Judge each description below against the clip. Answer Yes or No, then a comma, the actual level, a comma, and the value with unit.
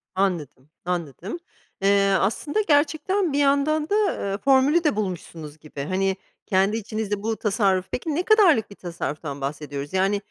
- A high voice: Yes, high, 200 Hz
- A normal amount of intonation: No, wide, 8.2 semitones